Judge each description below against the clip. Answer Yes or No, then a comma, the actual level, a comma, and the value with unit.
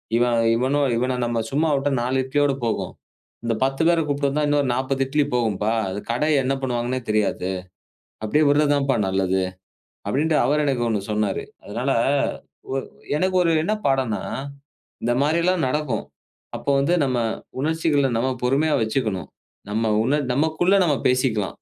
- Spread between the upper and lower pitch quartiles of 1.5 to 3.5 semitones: No, average, 3.9 semitones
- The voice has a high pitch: No, low, 135 Hz